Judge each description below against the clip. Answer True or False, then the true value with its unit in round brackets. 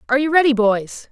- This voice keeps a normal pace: False (215 wpm)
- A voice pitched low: False (260 Hz)